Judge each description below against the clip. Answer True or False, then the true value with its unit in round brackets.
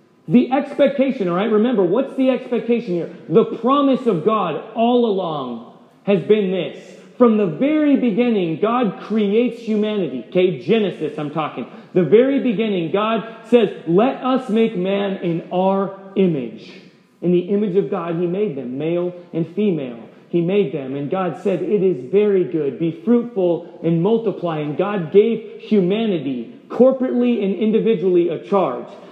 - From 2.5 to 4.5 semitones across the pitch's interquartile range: True (4.2 semitones)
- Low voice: False (200 Hz)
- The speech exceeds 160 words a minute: False (155 wpm)